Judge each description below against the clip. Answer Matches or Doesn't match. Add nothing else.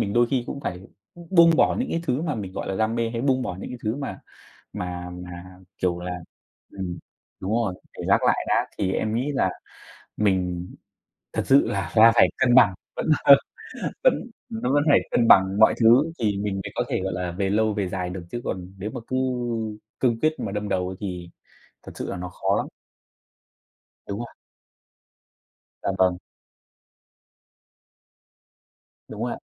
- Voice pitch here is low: Matches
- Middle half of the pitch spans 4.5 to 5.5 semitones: Matches